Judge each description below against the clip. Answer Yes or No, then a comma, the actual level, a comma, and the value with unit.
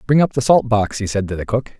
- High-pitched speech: No, low, 115 Hz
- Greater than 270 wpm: Yes, fast, 335 wpm